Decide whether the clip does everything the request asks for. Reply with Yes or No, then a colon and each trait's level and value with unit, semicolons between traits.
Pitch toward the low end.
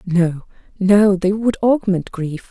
No: high, 190 Hz